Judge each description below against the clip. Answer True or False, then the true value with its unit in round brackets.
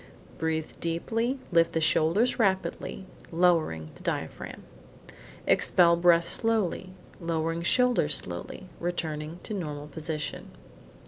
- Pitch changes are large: False (2.9 semitones)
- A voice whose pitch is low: False (170 Hz)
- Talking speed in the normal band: False (105 wpm)